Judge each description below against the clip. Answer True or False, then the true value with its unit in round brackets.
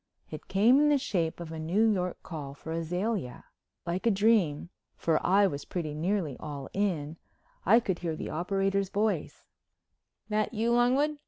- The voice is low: False (190 Hz)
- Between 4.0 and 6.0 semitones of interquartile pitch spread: True (5.1 semitones)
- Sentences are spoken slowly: False (165 wpm)